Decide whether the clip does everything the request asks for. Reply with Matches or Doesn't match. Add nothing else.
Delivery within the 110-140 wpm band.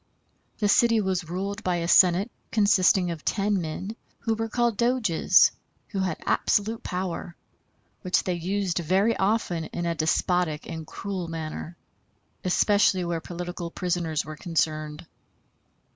Matches